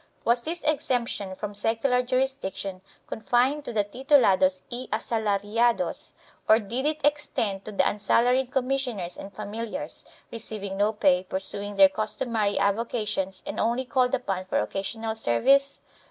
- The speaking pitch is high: Yes, high, 220 Hz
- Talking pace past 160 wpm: No, average, 140 wpm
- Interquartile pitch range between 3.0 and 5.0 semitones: Yes, average, 4.2 semitones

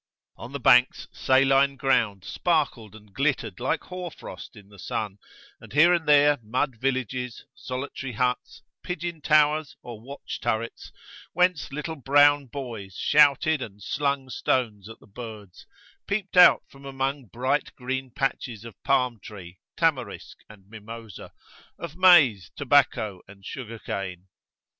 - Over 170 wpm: No, average, 140 wpm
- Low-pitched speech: Yes, low, 130 Hz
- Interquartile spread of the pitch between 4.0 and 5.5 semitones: Yes, average, 4.7 semitones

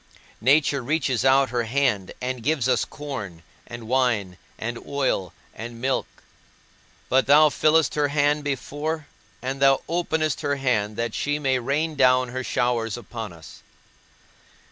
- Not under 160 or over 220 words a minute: No, average, 145 wpm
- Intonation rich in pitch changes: No, average, 3.5 semitones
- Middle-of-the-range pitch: No, low, 130 Hz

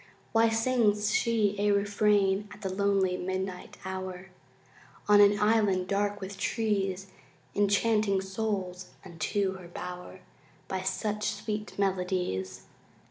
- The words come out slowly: Yes, slow, 115 wpm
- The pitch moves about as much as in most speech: No, narrow, 1.8 semitones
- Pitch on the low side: No, high, 200 Hz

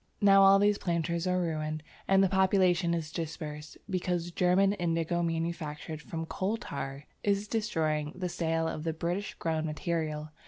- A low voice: No, medium, 170 Hz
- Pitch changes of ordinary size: Yes, average, 3.1 semitones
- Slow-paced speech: No, average, 155 wpm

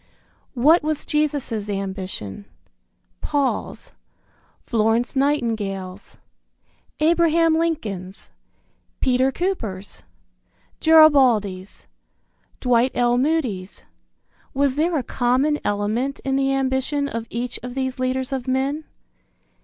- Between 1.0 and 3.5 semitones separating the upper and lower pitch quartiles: No, average, 4.9 semitones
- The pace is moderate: No, slow, 90 wpm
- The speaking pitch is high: Yes, very high, 260 Hz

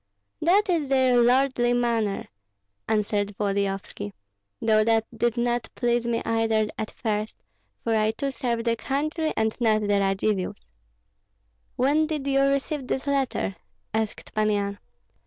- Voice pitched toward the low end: No, high, 230 Hz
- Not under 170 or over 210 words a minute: No, average, 140 wpm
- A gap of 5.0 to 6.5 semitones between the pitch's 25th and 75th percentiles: No, average, 3.8 semitones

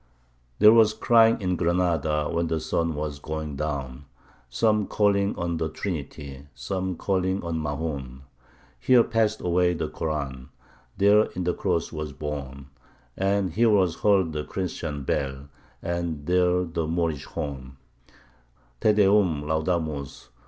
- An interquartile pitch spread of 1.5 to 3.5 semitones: No, average, 4.3 semitones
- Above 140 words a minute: No, slow, 135 wpm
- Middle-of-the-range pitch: No, very low, 85 Hz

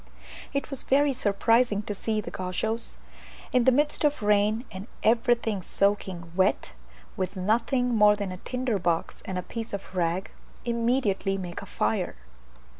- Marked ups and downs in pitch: No, average, 4.1 semitones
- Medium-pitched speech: No, high, 210 Hz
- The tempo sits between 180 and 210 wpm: No, average, 155 wpm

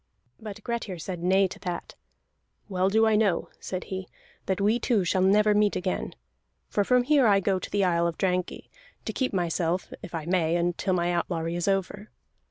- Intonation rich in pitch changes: No, average, 2.9 semitones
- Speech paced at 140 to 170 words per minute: No, average, 190 wpm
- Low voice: No, high, 190 Hz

